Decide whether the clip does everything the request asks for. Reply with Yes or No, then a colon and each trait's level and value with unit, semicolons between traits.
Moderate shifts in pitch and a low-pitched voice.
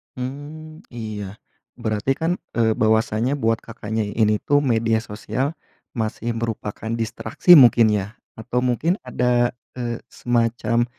No: narrow, 2.3 semitones; low, 115 Hz